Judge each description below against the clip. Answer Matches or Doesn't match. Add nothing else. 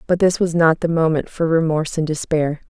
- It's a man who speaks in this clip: Doesn't match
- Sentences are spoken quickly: Matches